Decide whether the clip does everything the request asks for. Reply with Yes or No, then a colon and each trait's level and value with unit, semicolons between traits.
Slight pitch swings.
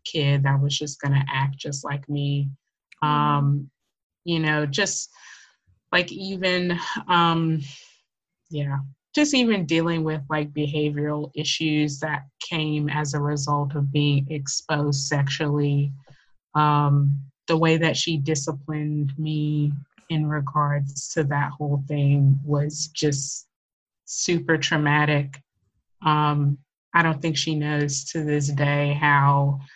Yes: narrow, 1.6 semitones